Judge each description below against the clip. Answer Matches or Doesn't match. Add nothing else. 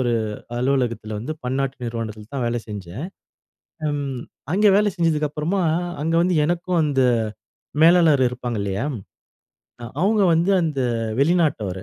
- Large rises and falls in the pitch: Matches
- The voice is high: Doesn't match